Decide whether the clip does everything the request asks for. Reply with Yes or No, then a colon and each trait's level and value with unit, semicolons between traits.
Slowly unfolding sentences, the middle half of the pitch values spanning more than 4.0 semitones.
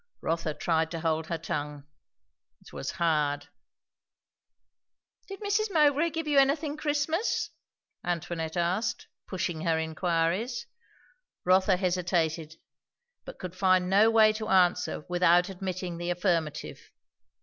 Yes: slow, 115 wpm; average, 5.3 semitones